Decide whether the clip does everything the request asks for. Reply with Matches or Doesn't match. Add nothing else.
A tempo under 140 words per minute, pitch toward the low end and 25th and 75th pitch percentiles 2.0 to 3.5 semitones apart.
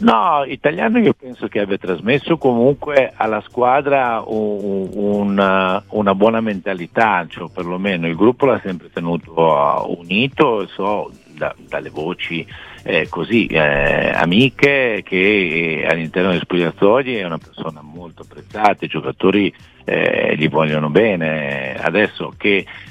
Doesn't match